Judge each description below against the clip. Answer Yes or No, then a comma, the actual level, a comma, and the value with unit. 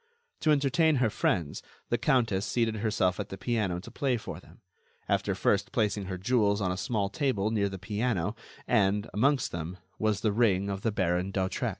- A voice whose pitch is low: Yes, low, 105 Hz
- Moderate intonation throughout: Yes, average, 3.7 semitones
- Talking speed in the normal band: Yes, average, 190 wpm